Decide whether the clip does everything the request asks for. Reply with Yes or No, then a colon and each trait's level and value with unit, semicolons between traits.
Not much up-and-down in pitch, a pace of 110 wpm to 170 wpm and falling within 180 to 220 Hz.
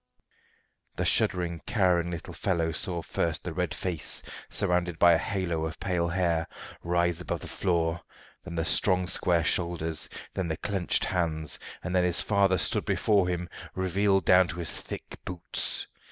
No: narrow, 1.7 semitones; average, 160 wpm; very low, 90 Hz